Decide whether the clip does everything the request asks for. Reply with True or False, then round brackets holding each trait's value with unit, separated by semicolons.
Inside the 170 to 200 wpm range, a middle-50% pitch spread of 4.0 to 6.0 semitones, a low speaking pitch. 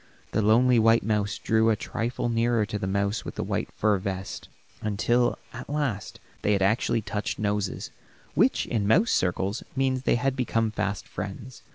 False (175 wpm; 2.8 semitones; 110 Hz)